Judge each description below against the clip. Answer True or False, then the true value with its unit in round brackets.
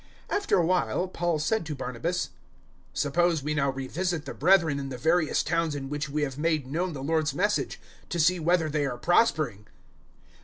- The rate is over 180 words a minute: True (190 wpm)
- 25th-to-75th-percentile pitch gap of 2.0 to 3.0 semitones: False (3.7 semitones)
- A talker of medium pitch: True (155 Hz)